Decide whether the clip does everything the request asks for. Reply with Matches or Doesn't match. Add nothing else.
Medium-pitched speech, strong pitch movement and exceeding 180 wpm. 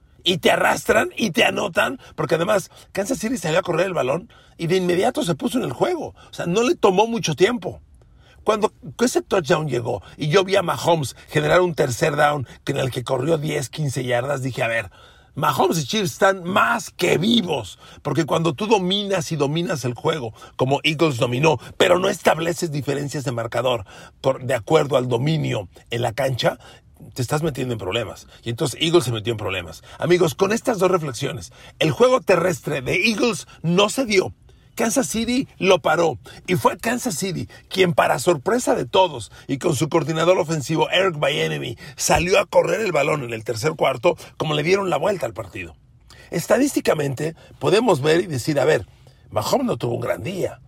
Matches